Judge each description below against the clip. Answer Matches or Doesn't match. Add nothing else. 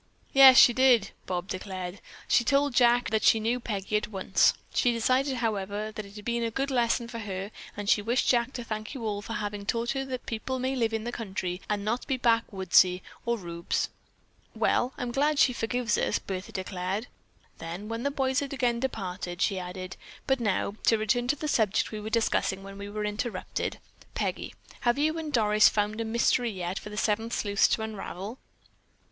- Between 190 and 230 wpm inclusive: Matches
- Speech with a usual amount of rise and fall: Matches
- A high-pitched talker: Matches